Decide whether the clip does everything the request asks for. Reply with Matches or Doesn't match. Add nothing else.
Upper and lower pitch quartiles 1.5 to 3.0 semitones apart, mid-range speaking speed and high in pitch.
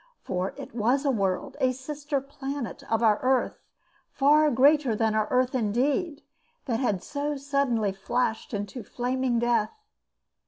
Doesn't match